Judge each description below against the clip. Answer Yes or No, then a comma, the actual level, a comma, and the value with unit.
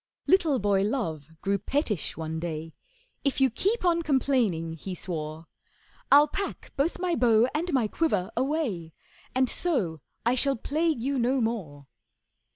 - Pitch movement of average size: No, wide, 8.8 semitones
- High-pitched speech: Yes, high, 240 Hz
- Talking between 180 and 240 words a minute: No, average, 150 wpm